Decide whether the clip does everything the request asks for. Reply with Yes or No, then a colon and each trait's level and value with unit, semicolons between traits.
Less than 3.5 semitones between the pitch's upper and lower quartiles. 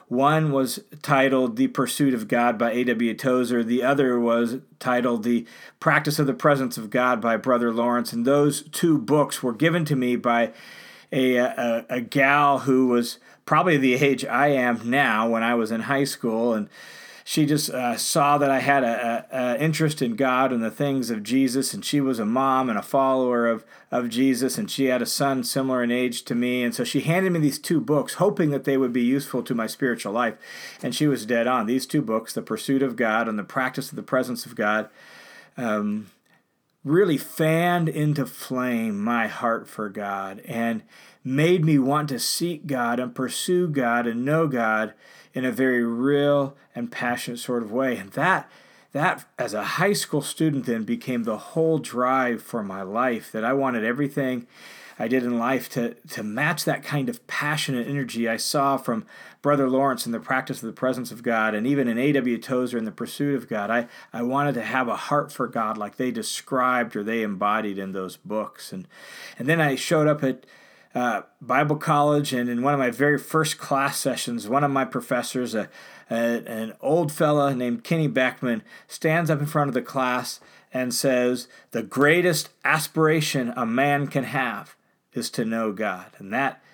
Yes: average, 3.1 semitones